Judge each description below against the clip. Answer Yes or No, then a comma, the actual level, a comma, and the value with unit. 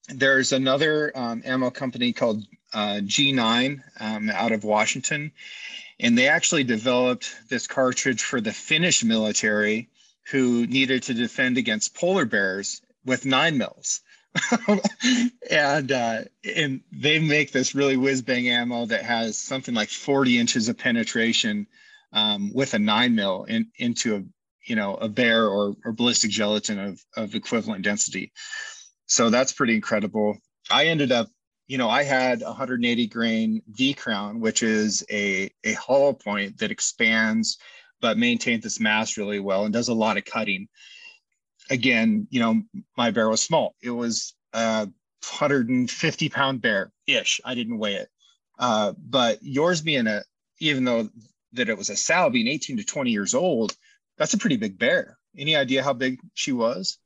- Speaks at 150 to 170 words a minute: Yes, average, 160 wpm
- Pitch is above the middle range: No, low, 130 Hz